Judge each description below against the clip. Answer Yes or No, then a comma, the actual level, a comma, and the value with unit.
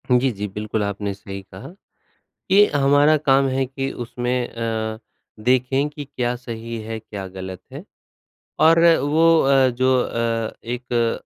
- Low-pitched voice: Yes, low, 120 Hz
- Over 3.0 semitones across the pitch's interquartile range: Yes, average, 3.6 semitones